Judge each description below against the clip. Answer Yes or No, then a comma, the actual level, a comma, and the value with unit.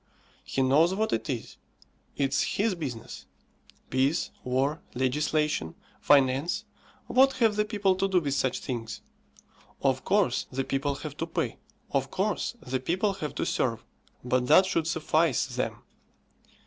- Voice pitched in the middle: Yes, medium, 150 Hz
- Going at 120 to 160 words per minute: Yes, average, 145 wpm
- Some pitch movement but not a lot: No, wide, 6.3 semitones